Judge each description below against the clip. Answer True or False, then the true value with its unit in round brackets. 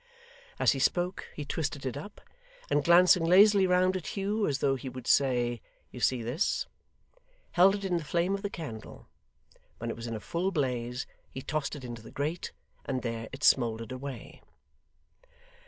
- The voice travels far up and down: True (6.5 semitones)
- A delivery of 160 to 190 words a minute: True (180 wpm)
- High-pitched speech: False (140 Hz)